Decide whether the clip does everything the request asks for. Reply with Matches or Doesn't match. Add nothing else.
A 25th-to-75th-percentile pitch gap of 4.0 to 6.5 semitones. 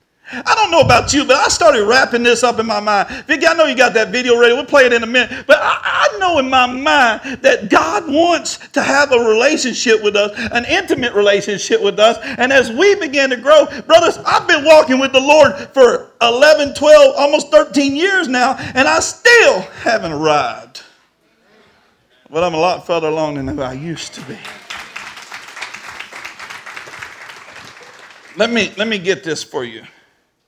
Matches